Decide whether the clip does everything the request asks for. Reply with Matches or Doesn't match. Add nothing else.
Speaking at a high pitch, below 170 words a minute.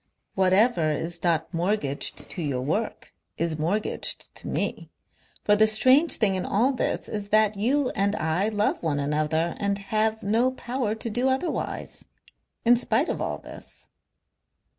Matches